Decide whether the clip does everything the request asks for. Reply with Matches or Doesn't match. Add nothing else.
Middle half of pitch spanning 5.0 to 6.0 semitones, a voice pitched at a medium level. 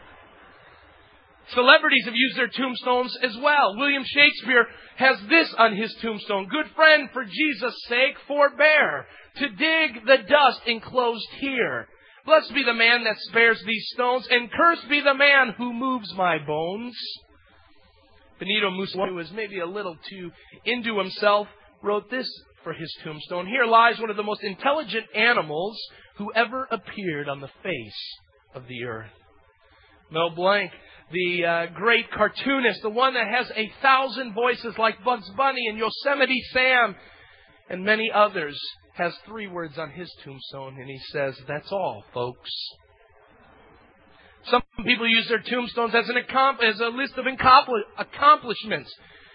Doesn't match